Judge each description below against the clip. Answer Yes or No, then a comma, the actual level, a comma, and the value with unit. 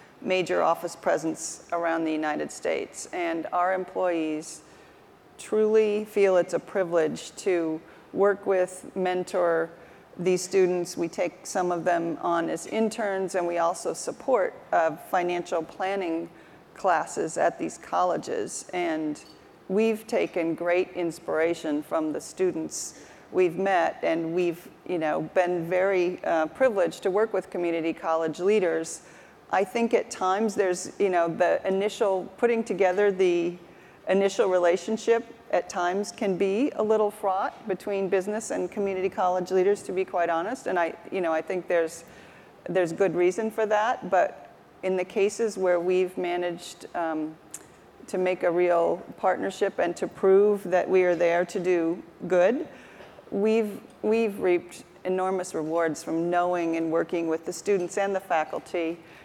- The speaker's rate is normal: Yes, average, 145 wpm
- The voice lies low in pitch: No, medium, 185 Hz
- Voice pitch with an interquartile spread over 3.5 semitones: No, average, 2.7 semitones